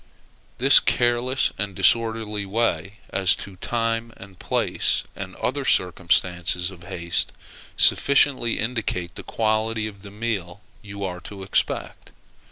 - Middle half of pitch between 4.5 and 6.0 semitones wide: No, average, 3.6 semitones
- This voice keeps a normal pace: No, slow, 125 wpm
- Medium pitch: No, low, 105 Hz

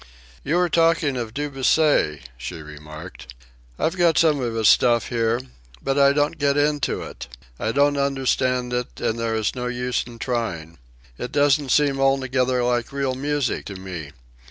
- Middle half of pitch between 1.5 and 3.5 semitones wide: No, average, 4.0 semitones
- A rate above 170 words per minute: No, average, 165 wpm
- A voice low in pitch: Yes, low, 125 Hz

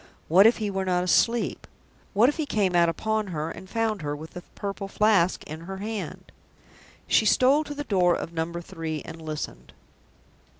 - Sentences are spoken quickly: No, average, 185 wpm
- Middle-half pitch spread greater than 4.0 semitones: Yes, average, 4.7 semitones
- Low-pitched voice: No, high, 190 Hz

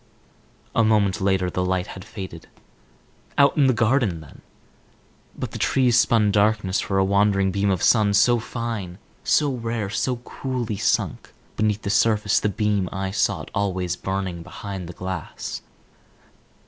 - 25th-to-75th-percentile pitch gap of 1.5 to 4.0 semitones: Yes, average, 3.1 semitones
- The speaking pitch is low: Yes, low, 100 Hz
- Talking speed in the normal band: Yes, average, 150 wpm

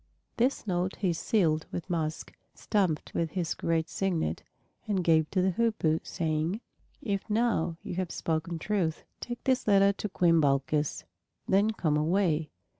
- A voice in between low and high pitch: Yes, medium, 175 Hz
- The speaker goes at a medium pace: Yes, average, 150 wpm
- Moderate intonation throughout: Yes, average, 3.9 semitones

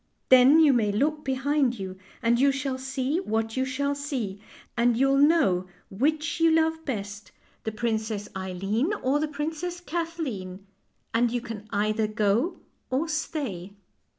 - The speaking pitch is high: Yes, very high, 260 Hz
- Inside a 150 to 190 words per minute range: Yes, average, 160 wpm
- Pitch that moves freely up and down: Yes, wide, 5.8 semitones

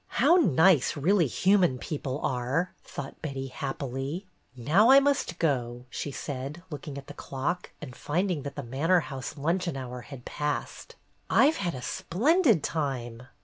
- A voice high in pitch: No, medium, 145 Hz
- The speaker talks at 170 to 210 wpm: No, average, 155 wpm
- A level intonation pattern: No, average, 5.1 semitones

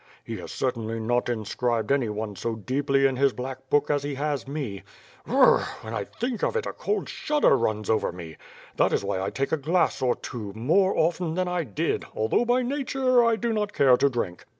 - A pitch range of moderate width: No, wide, 8.0 semitones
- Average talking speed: No, fast, 225 wpm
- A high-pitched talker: No, low, 135 Hz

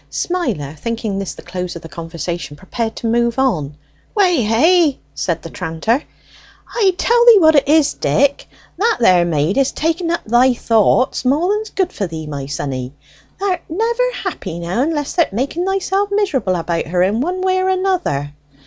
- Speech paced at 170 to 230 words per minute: Yes, average, 175 wpm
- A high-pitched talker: Yes, very high, 250 Hz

